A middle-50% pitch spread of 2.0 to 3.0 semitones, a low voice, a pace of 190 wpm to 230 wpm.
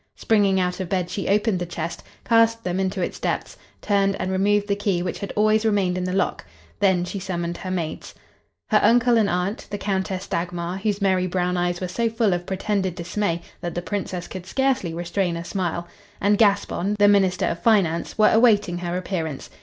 No: narrow, 2.6 semitones; high, 190 Hz; average, 200 wpm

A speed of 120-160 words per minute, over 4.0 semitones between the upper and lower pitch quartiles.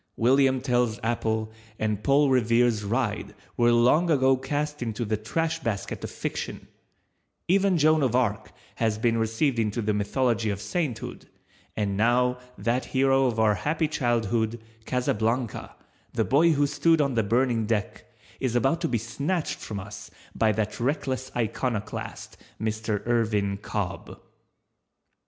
No: average, 140 wpm; average, 3.5 semitones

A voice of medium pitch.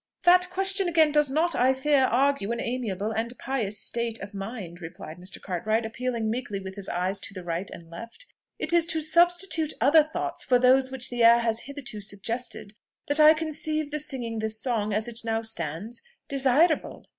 No: high, 240 Hz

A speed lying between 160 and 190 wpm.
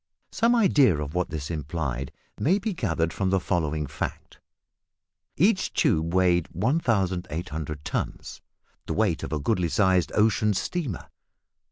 No: slow, 135 wpm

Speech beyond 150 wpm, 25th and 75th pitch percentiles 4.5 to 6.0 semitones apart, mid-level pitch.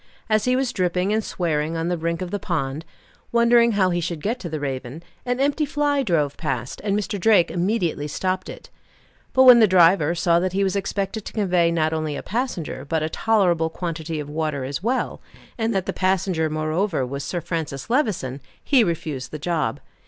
Yes: average, 200 wpm; average, 5.1 semitones; medium, 175 Hz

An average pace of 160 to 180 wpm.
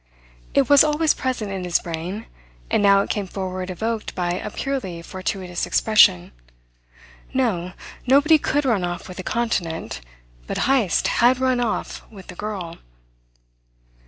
No: average, 145 wpm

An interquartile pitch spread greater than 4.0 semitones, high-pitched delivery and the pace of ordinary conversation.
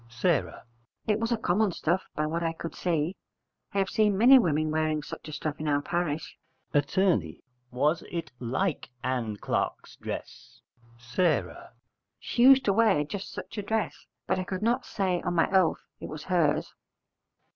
No: average, 4.9 semitones; medium, 170 Hz; average, 170 wpm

